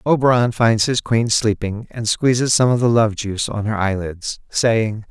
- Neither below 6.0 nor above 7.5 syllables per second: No, 4.5 syllables/s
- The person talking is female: No, male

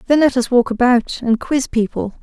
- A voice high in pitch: Yes, high, 245 Hz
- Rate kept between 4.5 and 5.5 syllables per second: Yes, 5.0 syllables/s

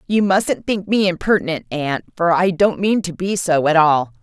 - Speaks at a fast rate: Yes, fast, 215 wpm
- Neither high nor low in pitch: Yes, medium, 180 Hz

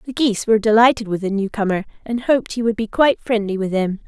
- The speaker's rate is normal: No, fast, 235 wpm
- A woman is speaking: Yes, female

